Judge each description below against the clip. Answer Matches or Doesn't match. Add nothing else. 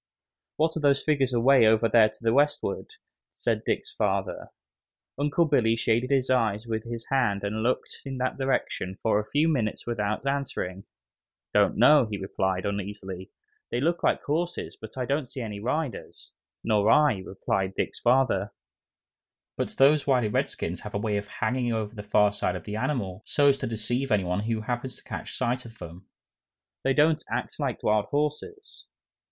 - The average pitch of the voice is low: Matches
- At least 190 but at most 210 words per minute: Doesn't match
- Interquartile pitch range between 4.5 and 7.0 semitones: Matches